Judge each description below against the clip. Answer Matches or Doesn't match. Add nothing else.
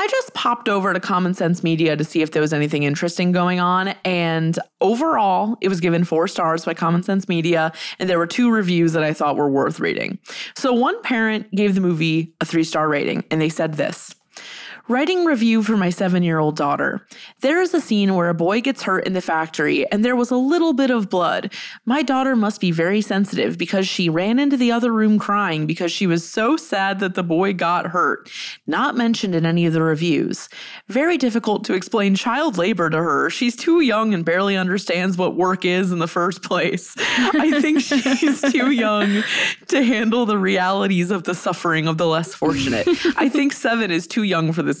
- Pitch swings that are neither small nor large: Doesn't match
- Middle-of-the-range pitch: Doesn't match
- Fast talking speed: Matches